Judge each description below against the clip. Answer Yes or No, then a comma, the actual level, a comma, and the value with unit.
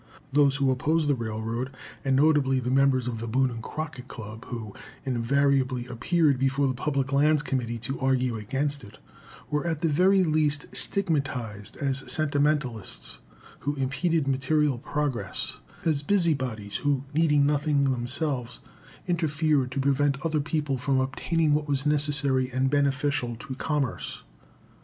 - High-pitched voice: No, medium, 140 Hz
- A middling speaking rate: Yes, average, 145 wpm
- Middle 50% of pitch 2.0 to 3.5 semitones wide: Yes, narrow, 2.6 semitones